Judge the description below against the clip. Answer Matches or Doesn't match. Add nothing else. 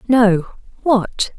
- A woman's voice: Matches